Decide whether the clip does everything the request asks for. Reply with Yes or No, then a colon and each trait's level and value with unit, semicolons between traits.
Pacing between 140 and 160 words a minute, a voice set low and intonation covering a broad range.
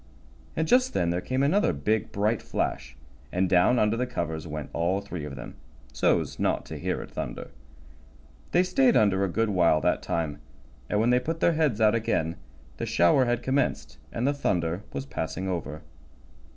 No: average, 185 wpm; low, 100 Hz; wide, 7.0 semitones